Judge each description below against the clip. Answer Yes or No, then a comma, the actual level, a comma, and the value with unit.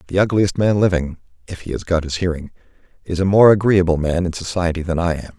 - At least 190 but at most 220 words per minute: Yes, average, 200 wpm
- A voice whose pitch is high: No, very low, 90 Hz